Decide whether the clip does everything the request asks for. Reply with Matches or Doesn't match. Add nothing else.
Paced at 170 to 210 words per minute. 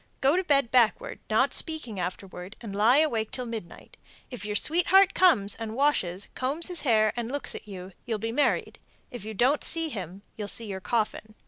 Matches